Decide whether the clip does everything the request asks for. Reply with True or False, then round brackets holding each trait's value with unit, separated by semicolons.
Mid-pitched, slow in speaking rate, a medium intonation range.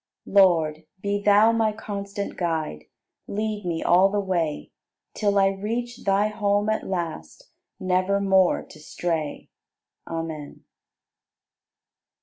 False (195 Hz; 115 wpm; 3.4 semitones)